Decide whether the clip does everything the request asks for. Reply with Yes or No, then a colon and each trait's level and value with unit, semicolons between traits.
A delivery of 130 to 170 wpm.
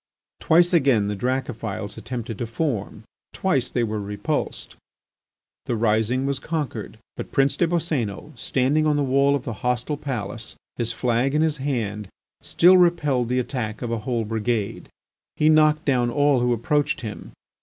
Yes: average, 160 wpm